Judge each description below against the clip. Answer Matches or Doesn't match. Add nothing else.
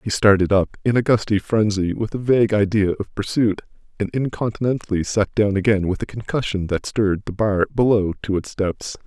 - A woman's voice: Doesn't match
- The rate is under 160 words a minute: Doesn't match